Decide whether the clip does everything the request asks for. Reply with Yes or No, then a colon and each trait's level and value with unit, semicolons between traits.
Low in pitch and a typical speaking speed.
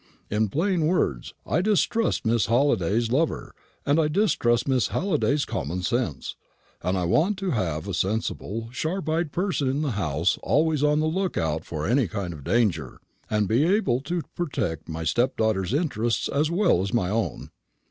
Yes: low, 120 Hz; average, 170 wpm